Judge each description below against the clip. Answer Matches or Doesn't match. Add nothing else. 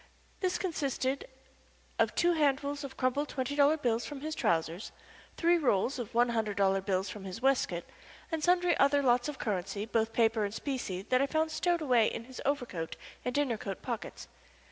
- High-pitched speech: Matches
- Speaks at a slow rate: Doesn't match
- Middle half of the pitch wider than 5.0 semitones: Matches